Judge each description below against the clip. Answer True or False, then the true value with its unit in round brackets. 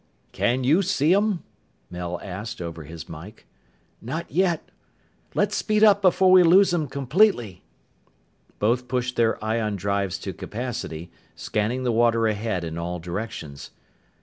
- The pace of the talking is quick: False (140 wpm)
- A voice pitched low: True (115 Hz)